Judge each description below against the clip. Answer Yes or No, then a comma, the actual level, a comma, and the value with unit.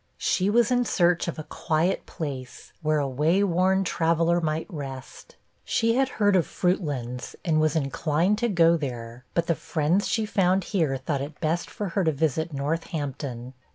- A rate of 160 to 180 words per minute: Yes, average, 175 wpm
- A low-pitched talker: No, medium, 165 Hz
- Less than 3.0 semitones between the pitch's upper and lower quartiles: No, average, 4.3 semitones